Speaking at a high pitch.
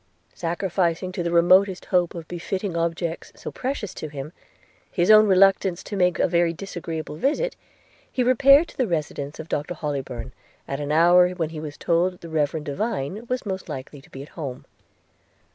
No: medium, 170 Hz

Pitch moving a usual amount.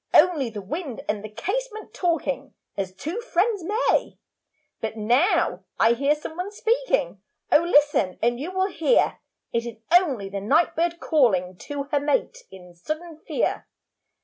No: wide, 7.9 semitones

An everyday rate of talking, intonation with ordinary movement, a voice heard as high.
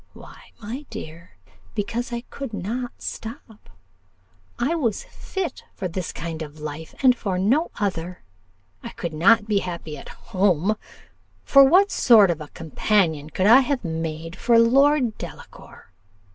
No: average, 145 wpm; wide, 6.6 semitones; high, 205 Hz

